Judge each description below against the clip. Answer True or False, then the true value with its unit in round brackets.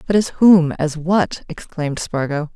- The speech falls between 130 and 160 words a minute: True (140 wpm)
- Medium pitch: True (165 Hz)